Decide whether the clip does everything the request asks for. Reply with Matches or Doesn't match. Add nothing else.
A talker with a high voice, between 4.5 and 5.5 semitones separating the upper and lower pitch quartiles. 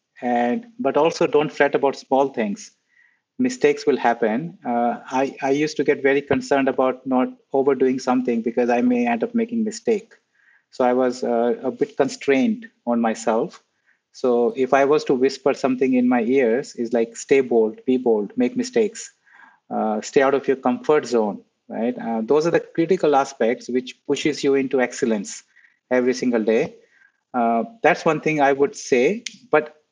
Doesn't match